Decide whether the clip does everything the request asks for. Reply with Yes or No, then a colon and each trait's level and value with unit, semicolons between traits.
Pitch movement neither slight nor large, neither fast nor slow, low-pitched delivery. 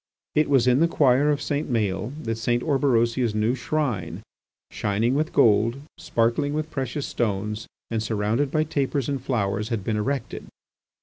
Yes: average, 4.4 semitones; average, 160 wpm; low, 120 Hz